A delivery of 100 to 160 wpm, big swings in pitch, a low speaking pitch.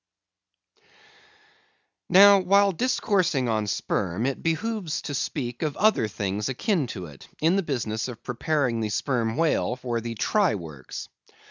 Yes: average, 140 wpm; wide, 8.1 semitones; low, 130 Hz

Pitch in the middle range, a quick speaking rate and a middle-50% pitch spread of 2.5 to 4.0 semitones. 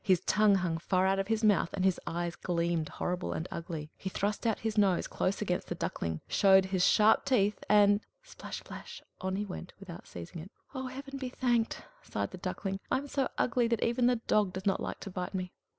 No: high, 195 Hz; fast, 220 wpm; average, 3.6 semitones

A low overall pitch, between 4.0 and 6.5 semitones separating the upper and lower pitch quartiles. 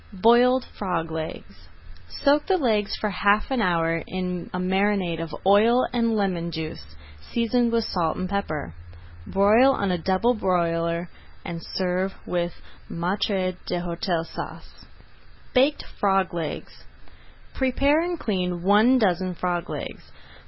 No: high, 190 Hz; average, 4.7 semitones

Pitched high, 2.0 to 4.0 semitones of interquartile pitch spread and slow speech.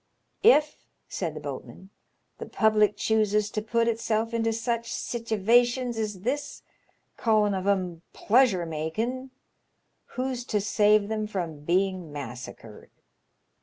Yes: high, 215 Hz; average, 3.7 semitones; slow, 120 wpm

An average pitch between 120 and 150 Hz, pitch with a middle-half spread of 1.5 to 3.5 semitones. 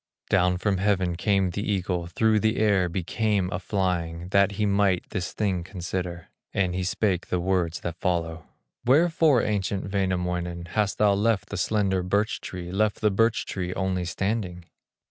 No: very low, 95 Hz; narrow, 2.6 semitones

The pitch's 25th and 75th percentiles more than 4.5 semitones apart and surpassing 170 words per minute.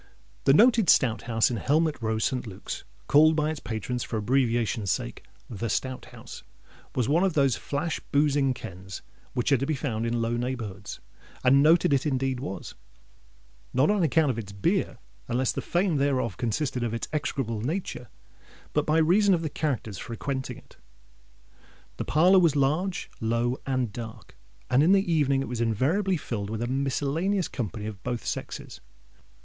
No: average, 4.9 semitones; average, 165 wpm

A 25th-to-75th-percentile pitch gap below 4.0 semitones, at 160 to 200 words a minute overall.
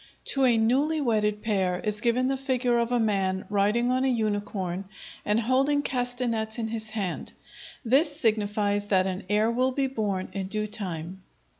Yes: average, 3.5 semitones; average, 170 wpm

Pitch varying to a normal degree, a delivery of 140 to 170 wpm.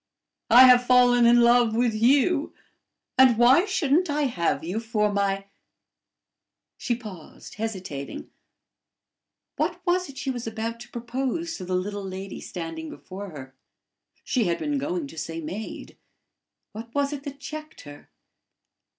No: wide, 5.7 semitones; average, 150 wpm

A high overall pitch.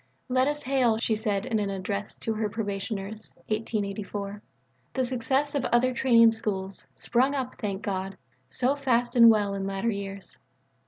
Yes: high, 220 Hz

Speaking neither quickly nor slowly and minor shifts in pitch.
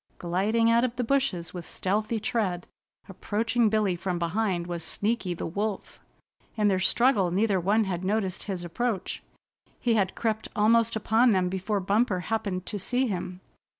No: average, 160 wpm; average, 3.6 semitones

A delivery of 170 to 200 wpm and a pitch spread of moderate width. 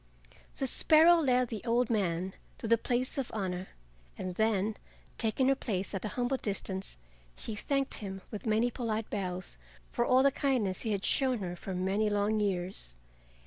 Yes: average, 175 wpm; average, 4.5 semitones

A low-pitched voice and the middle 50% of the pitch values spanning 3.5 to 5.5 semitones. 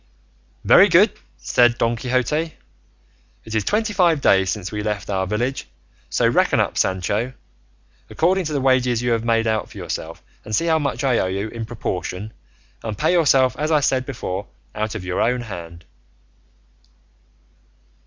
Yes: low, 115 Hz; average, 4.8 semitones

